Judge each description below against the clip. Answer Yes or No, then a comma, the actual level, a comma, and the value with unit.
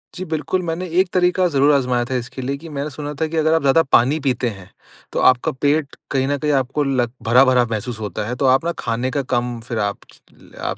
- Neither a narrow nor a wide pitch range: Yes, average, 3.7 semitones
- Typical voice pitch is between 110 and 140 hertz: Yes, low, 135 Hz